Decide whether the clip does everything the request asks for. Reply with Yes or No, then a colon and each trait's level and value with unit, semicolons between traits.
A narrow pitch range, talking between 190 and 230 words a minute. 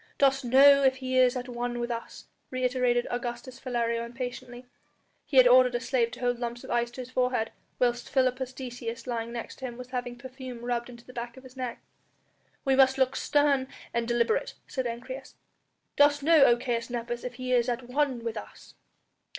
Yes: narrow, 1.5 semitones; average, 195 wpm